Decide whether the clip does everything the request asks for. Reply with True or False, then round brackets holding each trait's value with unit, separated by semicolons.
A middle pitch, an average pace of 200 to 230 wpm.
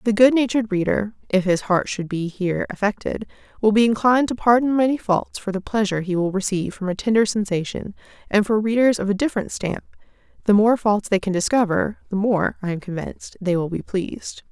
False (205 Hz; 205 wpm)